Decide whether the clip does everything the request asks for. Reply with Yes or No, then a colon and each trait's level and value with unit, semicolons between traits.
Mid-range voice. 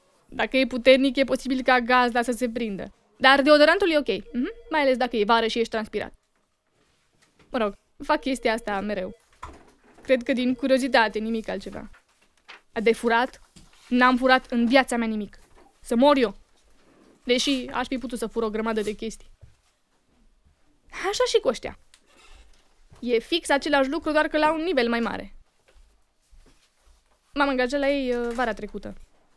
No: very high, 250 Hz